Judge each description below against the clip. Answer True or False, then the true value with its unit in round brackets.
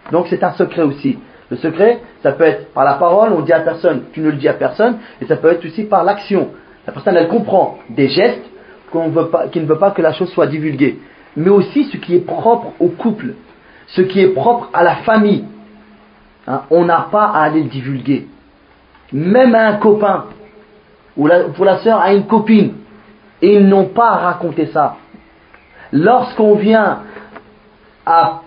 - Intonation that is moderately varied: True (4.7 semitones)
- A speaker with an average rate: True (195 wpm)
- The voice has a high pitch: True (195 Hz)